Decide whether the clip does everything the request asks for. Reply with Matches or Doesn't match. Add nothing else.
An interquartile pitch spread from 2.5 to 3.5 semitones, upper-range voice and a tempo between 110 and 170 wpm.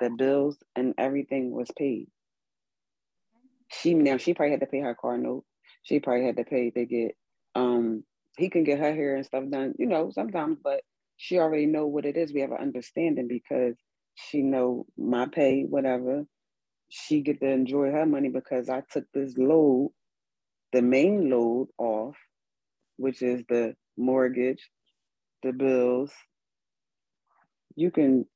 Doesn't match